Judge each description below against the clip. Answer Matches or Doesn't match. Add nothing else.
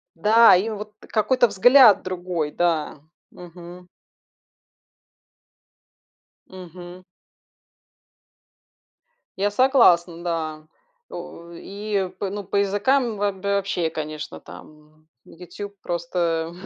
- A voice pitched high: Doesn't match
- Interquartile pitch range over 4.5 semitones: Doesn't match